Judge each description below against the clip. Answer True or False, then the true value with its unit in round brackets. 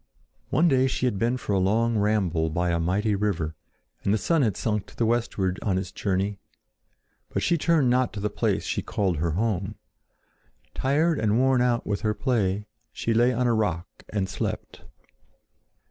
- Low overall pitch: True (105 Hz)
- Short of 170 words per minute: False (185 wpm)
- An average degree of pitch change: True (4.4 semitones)